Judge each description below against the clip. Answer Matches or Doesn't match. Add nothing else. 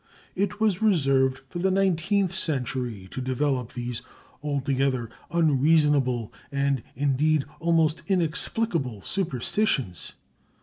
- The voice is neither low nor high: Matches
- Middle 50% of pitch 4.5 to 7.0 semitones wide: Matches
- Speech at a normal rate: Doesn't match